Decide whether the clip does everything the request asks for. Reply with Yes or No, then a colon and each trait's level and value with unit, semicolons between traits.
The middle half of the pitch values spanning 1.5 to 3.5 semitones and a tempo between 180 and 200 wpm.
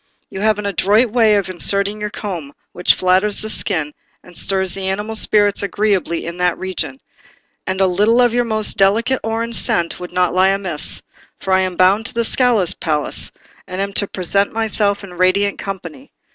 Yes: average, 2.7 semitones; average, 185 wpm